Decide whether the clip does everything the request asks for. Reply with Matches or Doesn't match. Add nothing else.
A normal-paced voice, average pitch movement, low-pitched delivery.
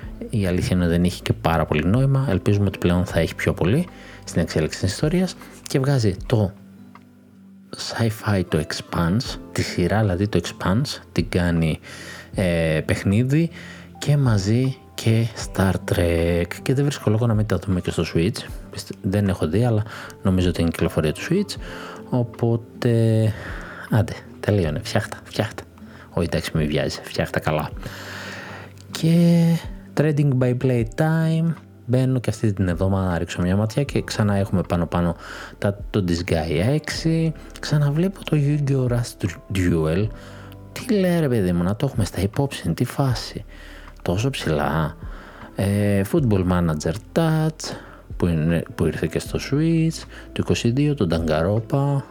Doesn't match